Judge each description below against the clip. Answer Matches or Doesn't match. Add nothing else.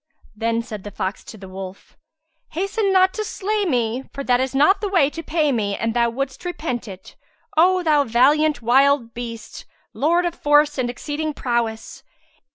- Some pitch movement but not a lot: Doesn't match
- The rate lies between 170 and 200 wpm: Matches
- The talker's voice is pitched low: Doesn't match